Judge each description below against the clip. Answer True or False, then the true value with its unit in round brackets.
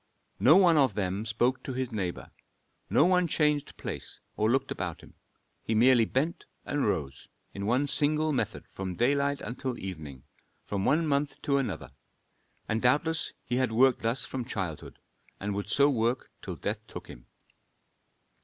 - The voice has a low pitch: True (125 Hz)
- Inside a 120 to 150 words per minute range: False (165 wpm)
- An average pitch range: False (5.7 semitones)